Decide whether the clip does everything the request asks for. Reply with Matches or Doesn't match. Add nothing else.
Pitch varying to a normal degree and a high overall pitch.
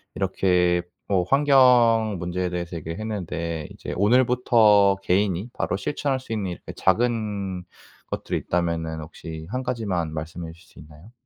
Doesn't match